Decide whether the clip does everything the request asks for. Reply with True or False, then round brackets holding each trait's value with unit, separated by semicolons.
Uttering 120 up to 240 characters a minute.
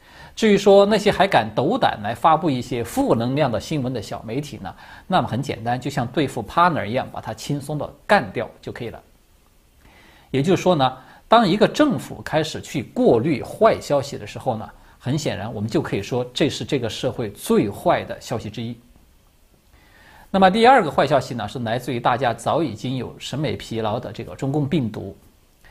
False (300 characters per minute)